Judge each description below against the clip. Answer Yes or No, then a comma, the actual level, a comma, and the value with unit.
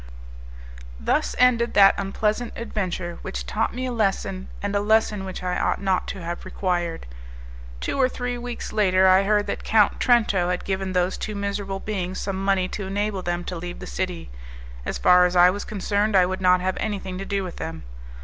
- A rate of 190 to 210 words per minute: Yes, average, 195 wpm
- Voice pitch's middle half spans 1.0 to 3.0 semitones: Yes, narrow, 2.5 semitones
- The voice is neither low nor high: No, high, 195 Hz